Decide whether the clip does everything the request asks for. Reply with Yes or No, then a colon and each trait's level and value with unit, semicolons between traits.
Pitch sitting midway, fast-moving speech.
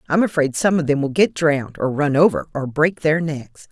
Yes: medium, 155 Hz; fast, 245 wpm